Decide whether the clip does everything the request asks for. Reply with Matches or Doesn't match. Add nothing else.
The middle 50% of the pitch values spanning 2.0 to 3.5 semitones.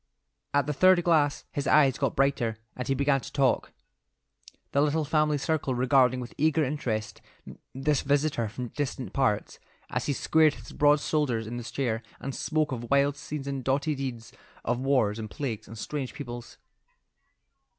Matches